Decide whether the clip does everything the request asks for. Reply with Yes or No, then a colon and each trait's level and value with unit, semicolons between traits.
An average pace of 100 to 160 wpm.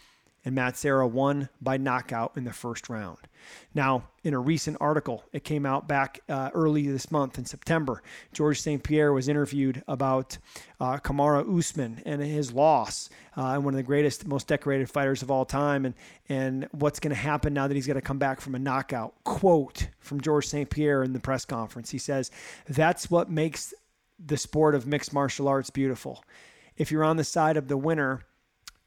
No: average, 195 wpm